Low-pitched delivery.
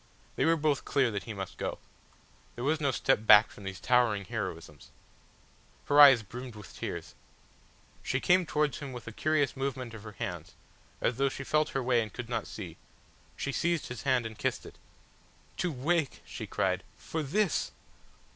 Yes: low, 130 Hz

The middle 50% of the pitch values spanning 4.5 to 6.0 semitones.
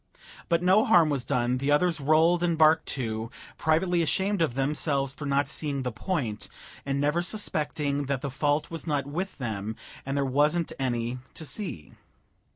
No: average, 3.7 semitones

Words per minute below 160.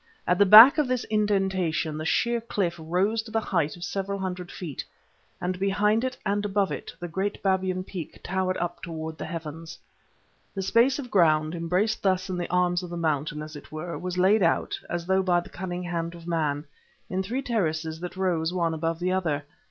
No: fast, 205 wpm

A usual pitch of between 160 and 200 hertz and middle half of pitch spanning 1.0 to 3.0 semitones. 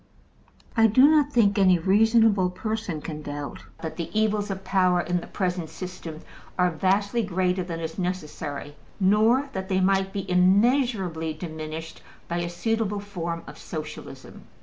No: medium, 185 Hz; average, 3.7 semitones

